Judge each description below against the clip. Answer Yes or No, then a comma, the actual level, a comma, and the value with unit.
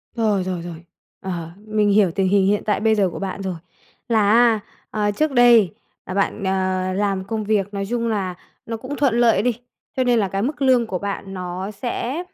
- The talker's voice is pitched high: Yes, high, 205 Hz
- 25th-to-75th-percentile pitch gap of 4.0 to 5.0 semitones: No, average, 3.3 semitones